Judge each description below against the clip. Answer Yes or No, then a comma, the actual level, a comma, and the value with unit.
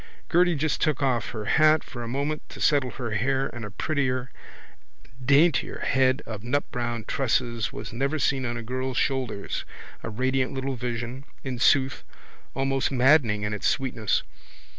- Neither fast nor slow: Yes, average, 160 wpm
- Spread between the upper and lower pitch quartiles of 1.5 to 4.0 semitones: Yes, narrow, 2.6 semitones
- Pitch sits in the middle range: No, low, 130 Hz